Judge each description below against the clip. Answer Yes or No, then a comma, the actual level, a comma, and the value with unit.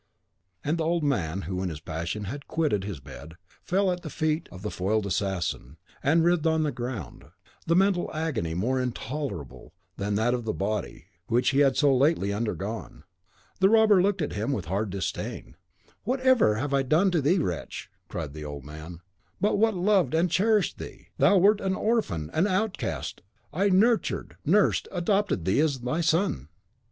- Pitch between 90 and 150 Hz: Yes, medium, 140 Hz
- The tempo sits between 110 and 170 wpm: No, average, 185 wpm